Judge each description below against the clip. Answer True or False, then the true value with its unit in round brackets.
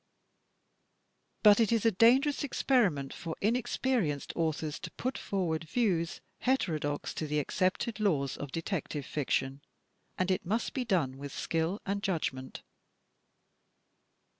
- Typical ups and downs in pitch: False (7.0 semitones)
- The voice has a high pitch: False (180 Hz)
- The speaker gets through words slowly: True (130 wpm)